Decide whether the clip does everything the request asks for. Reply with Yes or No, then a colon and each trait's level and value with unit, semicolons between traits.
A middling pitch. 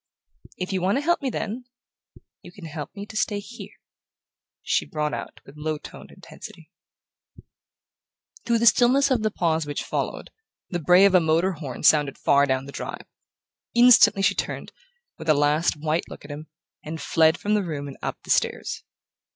Yes: medium, 170 Hz